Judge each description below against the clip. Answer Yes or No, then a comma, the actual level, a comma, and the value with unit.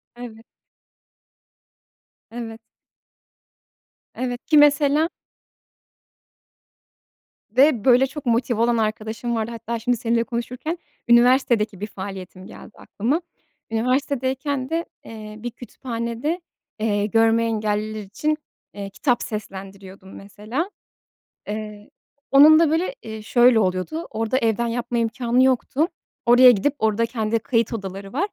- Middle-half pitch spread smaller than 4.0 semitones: Yes, average, 3.2 semitones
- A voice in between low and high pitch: No, high, 235 Hz